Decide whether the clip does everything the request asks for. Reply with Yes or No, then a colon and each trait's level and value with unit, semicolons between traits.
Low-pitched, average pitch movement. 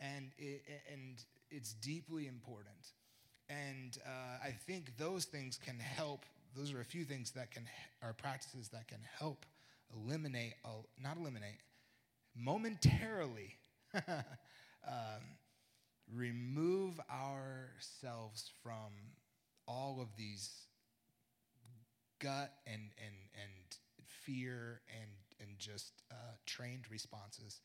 Yes: low, 125 Hz; average, 3.5 semitones